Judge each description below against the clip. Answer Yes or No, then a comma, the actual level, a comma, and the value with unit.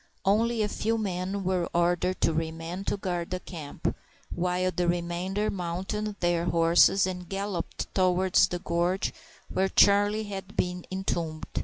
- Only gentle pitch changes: Yes, narrow, 2.2 semitones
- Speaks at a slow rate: No, average, 145 wpm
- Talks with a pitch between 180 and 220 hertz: Yes, medium, 185 Hz